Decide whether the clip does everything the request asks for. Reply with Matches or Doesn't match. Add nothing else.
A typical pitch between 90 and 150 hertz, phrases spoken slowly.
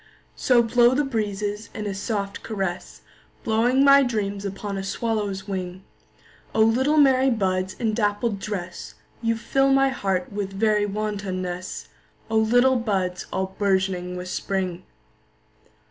Doesn't match